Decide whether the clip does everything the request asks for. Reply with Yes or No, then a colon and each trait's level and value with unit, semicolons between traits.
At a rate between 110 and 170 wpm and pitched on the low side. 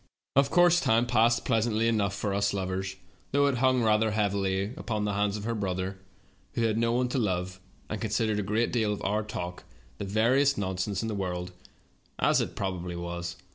No: average, 195 wpm; low, 105 Hz